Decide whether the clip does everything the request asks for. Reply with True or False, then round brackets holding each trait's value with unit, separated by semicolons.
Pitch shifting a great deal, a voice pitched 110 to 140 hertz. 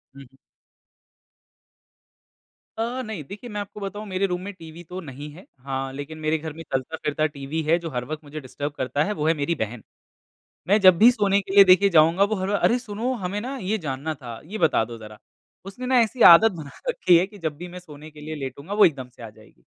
False (5.8 semitones; 165 Hz)